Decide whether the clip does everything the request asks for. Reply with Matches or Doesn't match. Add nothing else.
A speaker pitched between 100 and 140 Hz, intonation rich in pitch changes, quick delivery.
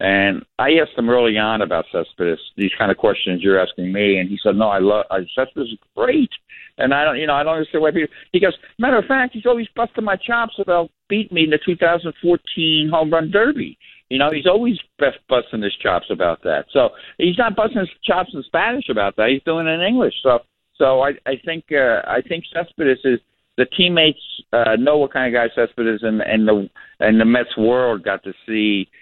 Doesn't match